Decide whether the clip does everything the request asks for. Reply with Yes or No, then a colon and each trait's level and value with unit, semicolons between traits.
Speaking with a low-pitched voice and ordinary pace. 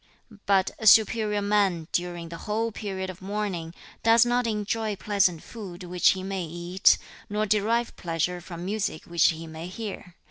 No: high, 195 Hz; average, 165 wpm